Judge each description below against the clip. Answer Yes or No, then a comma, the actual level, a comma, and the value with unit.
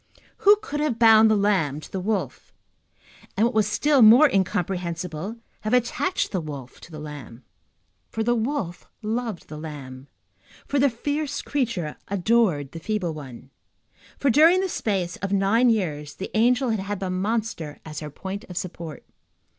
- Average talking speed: Yes, average, 165 wpm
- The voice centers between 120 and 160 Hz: No, high, 200 Hz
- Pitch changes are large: Yes, wide, 6.4 semitones